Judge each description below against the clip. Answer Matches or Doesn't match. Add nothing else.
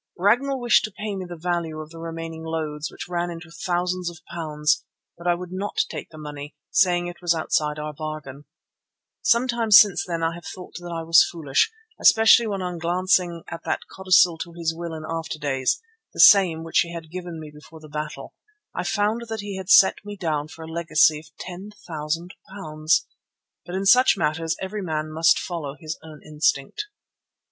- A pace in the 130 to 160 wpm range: Doesn't match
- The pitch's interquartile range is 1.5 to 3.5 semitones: Matches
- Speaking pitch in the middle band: Matches